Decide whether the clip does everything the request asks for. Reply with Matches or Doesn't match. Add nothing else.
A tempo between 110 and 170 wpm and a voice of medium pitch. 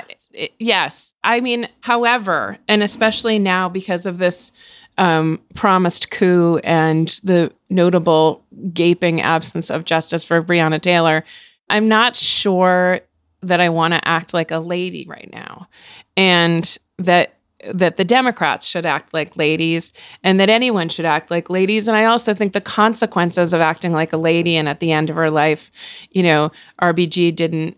Matches